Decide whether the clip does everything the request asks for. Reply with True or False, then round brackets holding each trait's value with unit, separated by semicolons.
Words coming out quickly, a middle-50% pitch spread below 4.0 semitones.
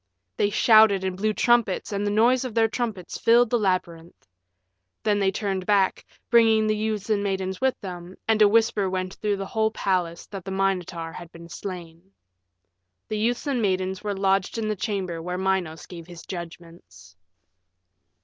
False (175 wpm; 3.1 semitones)